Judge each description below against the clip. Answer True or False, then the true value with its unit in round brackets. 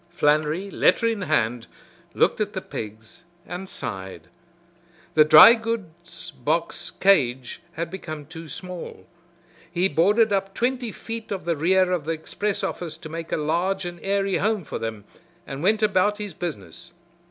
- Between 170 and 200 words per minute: False (155 wpm)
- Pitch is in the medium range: True (175 Hz)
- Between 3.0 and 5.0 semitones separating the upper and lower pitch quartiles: True (4.5 semitones)